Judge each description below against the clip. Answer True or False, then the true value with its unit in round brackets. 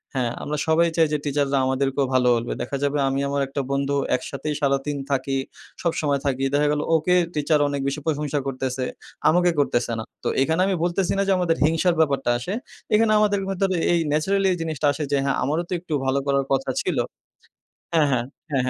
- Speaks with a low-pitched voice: False (145 Hz)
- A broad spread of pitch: False (3.2 semitones)